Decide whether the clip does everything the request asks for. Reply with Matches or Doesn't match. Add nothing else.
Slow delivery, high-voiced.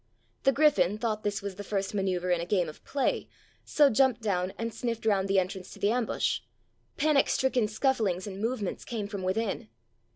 Doesn't match